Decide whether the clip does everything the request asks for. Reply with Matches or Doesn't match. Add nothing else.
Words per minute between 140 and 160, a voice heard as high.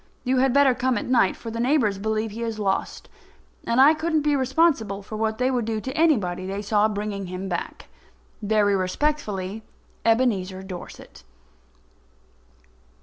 Matches